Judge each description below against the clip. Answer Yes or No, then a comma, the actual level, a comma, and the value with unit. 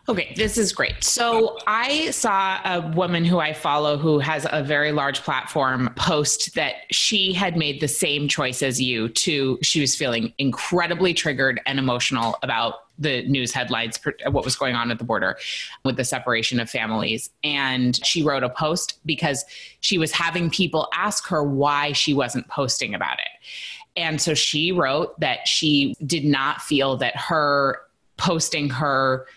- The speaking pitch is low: No, medium, 145 Hz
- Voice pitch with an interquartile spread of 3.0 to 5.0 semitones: Yes, average, 4.1 semitones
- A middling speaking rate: Yes, average, 170 wpm